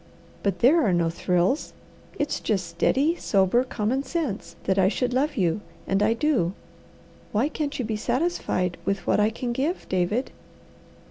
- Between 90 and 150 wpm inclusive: No, average, 160 wpm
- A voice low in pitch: No, high, 225 Hz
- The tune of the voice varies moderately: No, wide, 6.3 semitones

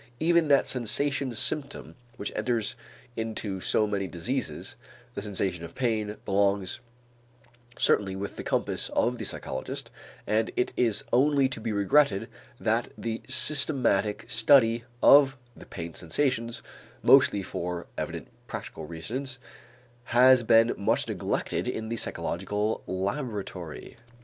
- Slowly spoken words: Yes, slow, 125 wpm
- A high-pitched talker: No, low, 110 Hz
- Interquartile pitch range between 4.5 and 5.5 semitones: Yes, average, 4.8 semitones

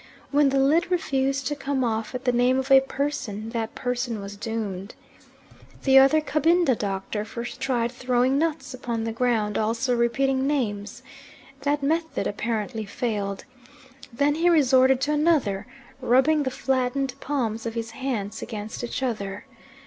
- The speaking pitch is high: Yes, very high, 250 Hz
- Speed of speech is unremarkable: Yes, average, 150 wpm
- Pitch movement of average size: Yes, average, 3.6 semitones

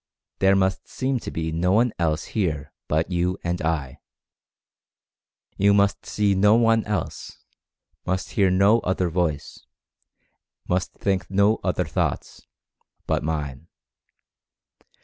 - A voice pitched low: Yes, very low, 95 Hz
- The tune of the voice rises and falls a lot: No, average, 3.6 semitones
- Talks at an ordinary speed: No, slow, 125 wpm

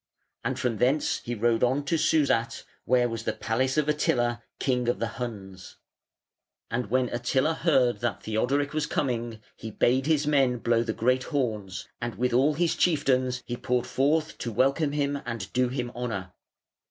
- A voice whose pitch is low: Yes, low, 125 Hz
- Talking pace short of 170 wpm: No, average, 175 wpm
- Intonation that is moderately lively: Yes, average, 3.2 semitones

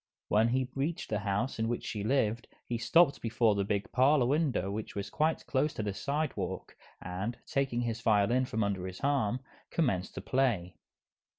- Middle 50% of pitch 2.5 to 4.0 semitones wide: No, average, 4.8 semitones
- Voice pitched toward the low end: Yes, low, 115 Hz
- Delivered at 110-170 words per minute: No, average, 180 wpm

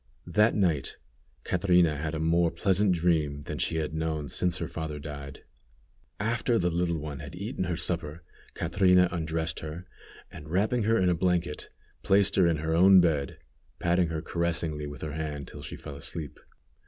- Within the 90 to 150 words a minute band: No, average, 175 wpm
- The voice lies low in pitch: Yes, very low, 85 Hz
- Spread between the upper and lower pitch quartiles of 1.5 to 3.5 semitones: Yes, average, 2.7 semitones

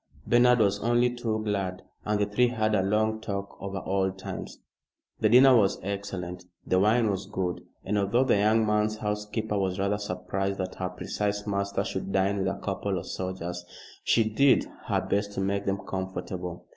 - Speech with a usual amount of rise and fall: No, narrow, 2.1 semitones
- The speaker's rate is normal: Yes, average, 185 wpm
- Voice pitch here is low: Yes, low, 100 Hz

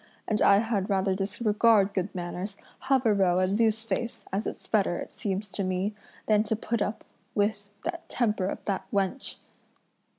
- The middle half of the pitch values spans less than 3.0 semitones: Yes, narrow, 2.4 semitones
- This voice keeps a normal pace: Yes, average, 175 wpm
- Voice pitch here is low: No, high, 205 Hz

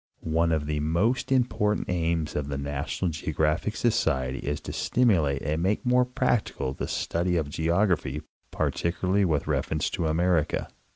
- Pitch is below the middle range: Yes, very low, 80 Hz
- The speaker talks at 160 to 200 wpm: No, average, 150 wpm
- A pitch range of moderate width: Yes, average, 4.6 semitones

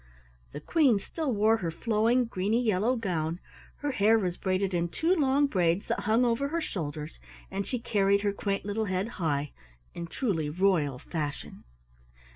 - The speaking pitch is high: Yes, high, 200 Hz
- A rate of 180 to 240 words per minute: No, average, 165 wpm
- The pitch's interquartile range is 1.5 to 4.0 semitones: No, average, 5.2 semitones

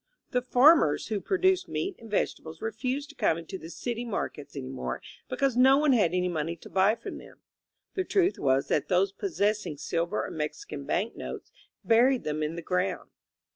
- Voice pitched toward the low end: No, high, 200 Hz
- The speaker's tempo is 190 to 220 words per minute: Yes, average, 195 wpm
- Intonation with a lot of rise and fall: Yes, wide, 8.2 semitones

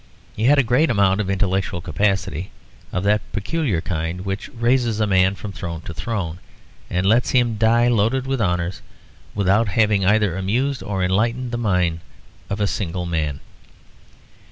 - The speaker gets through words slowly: No, average, 160 wpm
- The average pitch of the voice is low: Yes, low, 100 Hz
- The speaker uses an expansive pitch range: No, average, 4.0 semitones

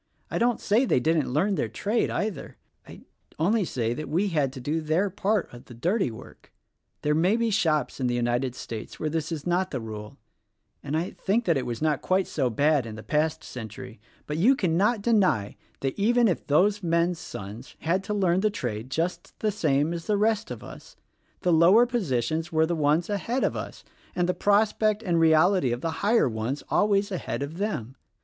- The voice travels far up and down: Yes, wide, 6.8 semitones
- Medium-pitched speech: Yes, medium, 165 Hz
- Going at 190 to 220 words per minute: Yes, average, 200 wpm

